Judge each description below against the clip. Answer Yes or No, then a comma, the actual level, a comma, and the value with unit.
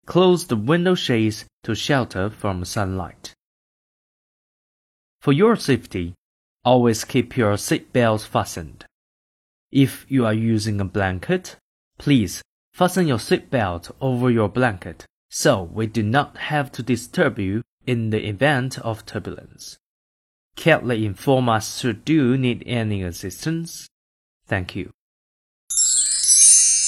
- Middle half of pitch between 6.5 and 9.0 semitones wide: No, average, 5.2 semitones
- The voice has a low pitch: Yes, low, 115 Hz